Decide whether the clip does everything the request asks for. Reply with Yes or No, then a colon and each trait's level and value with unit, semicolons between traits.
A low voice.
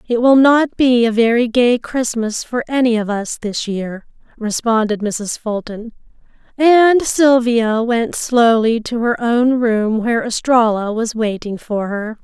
No: high, 230 Hz